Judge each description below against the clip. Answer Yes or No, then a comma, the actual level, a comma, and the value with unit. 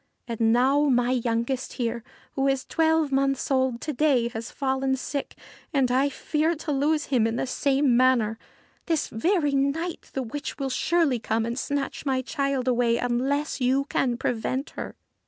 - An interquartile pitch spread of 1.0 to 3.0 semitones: Yes, average, 2.7 semitones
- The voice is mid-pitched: No, very high, 265 Hz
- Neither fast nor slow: Yes, average, 170 wpm